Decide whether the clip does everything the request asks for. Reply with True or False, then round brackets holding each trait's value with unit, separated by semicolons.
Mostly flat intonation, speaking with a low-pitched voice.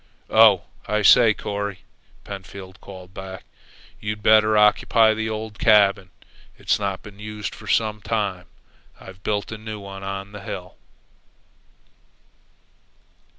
True (1.7 semitones; 105 Hz)